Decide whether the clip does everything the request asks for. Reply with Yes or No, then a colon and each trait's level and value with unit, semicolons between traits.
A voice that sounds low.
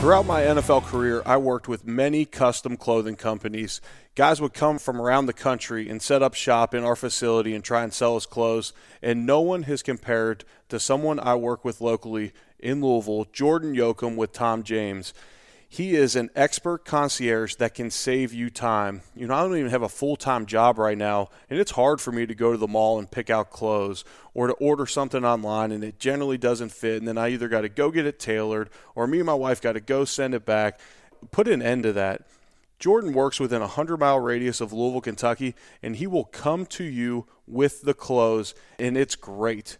Yes: low, 120 Hz